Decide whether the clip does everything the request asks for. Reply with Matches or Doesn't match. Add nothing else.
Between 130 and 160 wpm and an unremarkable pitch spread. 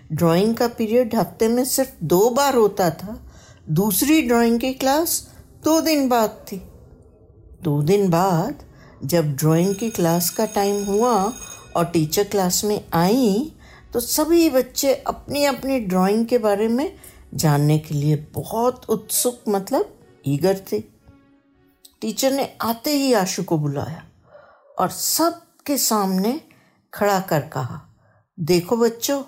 Doesn't match